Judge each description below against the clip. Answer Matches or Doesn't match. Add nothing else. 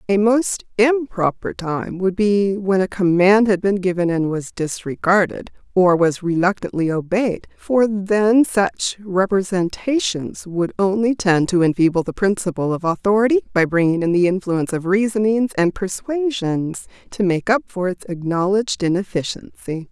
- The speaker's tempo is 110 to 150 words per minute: Matches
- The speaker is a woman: Matches